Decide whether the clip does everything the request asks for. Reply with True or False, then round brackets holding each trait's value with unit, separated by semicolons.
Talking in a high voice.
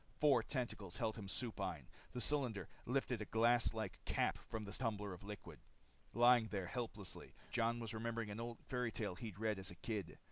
False (110 Hz)